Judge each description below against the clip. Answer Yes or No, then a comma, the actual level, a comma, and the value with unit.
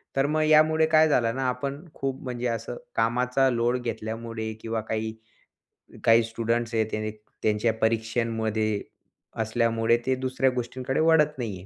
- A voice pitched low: Yes, low, 115 Hz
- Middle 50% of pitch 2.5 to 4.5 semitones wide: Yes, average, 2.8 semitones